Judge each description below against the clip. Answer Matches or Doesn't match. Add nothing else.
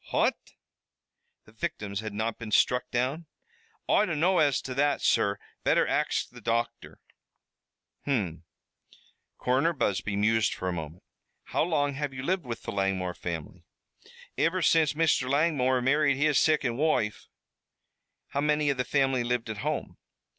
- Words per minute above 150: Doesn't match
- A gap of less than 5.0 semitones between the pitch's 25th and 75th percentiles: Doesn't match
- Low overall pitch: Matches